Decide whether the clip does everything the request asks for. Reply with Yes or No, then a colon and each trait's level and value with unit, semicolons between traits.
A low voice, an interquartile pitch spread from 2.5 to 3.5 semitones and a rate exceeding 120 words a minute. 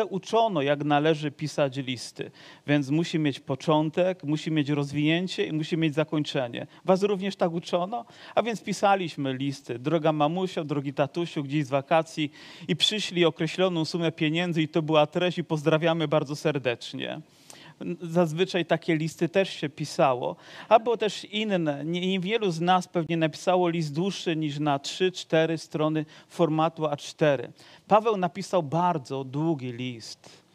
No: medium, 160 Hz; average, 3.0 semitones; average, 140 wpm